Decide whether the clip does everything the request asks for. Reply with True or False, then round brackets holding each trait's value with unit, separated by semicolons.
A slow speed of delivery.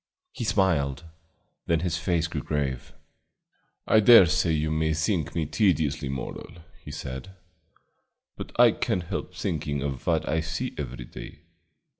False (145 wpm)